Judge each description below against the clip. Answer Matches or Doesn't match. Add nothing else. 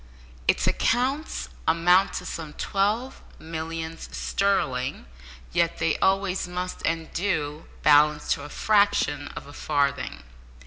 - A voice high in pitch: Doesn't match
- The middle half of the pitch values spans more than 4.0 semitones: Matches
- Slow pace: Matches